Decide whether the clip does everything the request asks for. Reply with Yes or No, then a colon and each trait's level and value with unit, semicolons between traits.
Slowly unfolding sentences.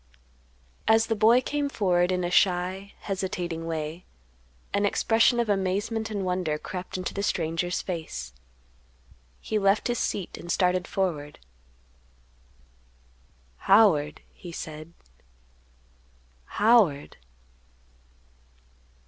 Yes: slow, 100 wpm